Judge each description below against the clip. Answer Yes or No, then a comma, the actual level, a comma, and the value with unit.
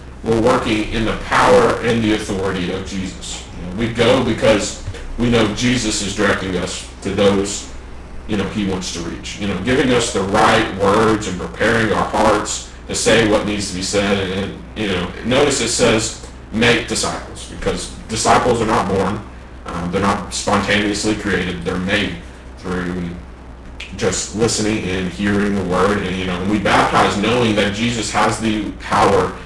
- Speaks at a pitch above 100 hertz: No, very low, 95 Hz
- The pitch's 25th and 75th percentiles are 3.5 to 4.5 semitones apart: Yes, average, 3.8 semitones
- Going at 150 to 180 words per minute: Yes, average, 175 wpm